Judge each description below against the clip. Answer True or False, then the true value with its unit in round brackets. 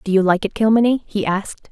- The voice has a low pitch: False (205 Hz)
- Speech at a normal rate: False (245 wpm)